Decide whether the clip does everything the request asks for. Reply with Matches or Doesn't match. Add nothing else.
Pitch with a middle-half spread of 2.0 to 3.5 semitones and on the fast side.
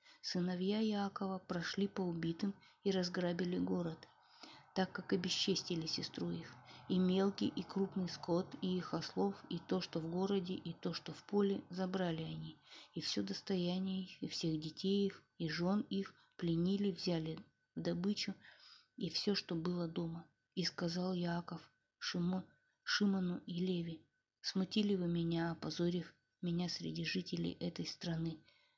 Doesn't match